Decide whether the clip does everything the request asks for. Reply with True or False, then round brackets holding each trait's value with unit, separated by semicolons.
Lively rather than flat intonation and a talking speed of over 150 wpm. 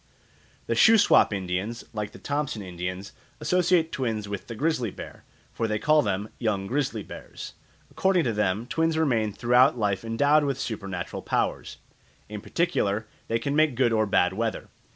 True (5.9 semitones; 160 wpm)